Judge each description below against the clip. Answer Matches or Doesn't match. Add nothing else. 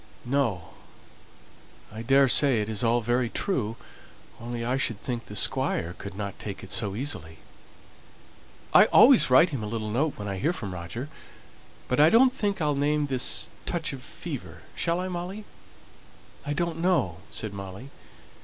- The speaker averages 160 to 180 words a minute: Matches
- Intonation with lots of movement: Matches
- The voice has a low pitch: Matches